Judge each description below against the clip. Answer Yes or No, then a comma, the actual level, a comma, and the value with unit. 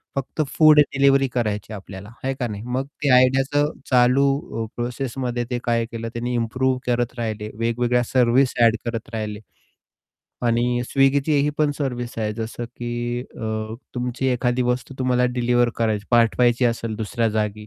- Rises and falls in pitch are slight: Yes, narrow, 2.3 semitones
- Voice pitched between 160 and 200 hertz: No, low, 120 Hz